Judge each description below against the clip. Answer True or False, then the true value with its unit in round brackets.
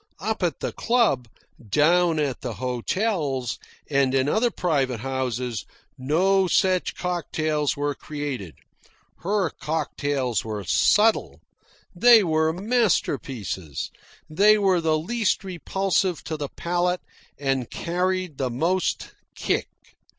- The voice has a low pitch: False (160 Hz)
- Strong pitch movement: True (5.8 semitones)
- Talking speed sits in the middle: False (115 wpm)